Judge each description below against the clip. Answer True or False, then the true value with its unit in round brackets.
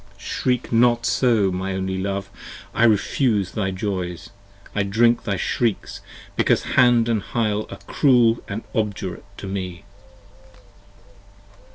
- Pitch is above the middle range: False (105 Hz)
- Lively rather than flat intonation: False (3.5 semitones)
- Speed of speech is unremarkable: False (130 wpm)